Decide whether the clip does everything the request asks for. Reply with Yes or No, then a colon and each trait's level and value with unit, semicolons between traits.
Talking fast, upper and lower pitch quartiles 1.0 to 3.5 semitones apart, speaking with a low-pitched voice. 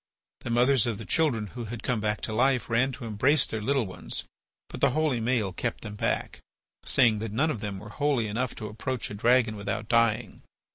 Yes: fast, 210 wpm; average, 3.2 semitones; low, 115 Hz